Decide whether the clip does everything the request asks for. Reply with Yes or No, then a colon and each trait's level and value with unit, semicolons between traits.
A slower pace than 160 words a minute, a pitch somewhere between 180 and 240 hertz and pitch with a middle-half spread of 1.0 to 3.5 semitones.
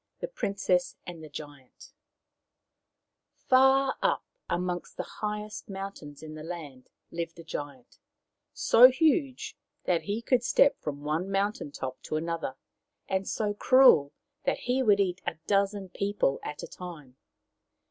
No: average, 140 wpm; medium, 185 Hz; wide, 5.5 semitones